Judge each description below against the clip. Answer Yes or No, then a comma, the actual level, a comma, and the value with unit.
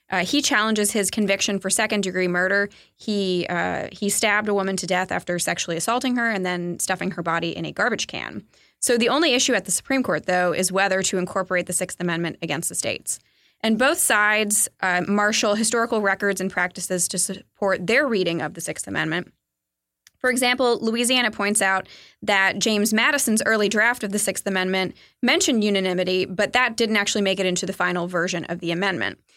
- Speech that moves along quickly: No, average, 195 wpm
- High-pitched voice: Yes, high, 195 Hz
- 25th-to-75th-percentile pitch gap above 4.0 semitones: No, average, 3.1 semitones